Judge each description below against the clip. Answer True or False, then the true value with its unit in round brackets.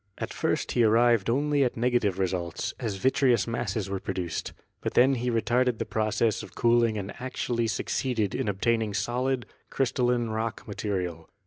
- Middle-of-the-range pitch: False (115 Hz)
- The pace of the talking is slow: False (155 wpm)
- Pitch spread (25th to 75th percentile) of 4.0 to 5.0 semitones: False (3.2 semitones)